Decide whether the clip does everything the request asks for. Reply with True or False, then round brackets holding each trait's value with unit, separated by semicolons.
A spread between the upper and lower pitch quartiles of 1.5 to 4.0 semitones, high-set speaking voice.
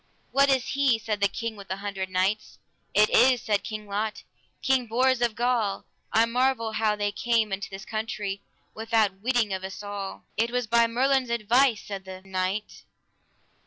True (3.1 semitones; 220 Hz)